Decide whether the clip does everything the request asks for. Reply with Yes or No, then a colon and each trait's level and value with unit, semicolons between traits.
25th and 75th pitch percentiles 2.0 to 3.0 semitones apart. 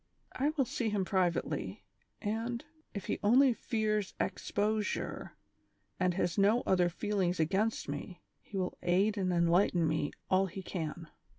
No: average, 3.5 semitones